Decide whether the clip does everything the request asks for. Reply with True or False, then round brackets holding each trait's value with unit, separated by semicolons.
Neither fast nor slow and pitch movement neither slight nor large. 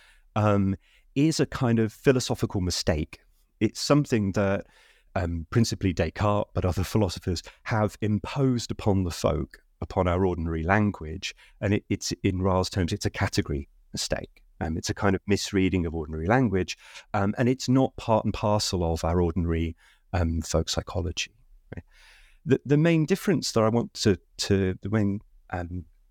True (160 wpm; 3.8 semitones)